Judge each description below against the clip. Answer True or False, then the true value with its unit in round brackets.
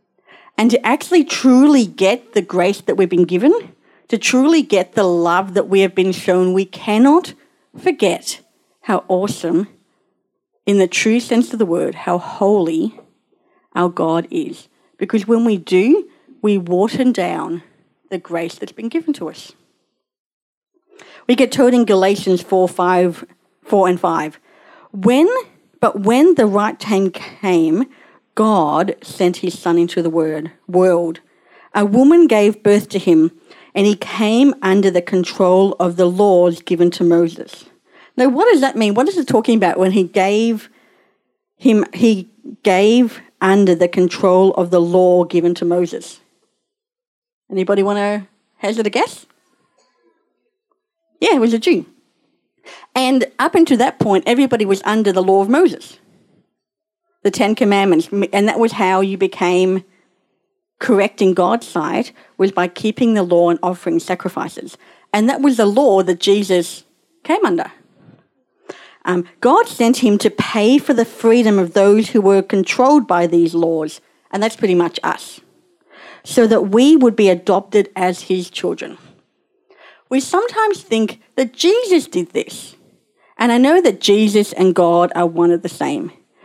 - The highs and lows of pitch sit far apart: True (6.1 semitones)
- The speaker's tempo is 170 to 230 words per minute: False (155 wpm)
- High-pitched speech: True (205 Hz)